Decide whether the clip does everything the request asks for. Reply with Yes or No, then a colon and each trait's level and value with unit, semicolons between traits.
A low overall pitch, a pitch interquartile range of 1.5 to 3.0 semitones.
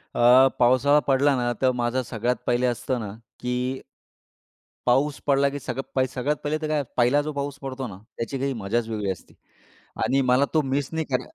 Yes: low, 130 Hz; narrow, 2.4 semitones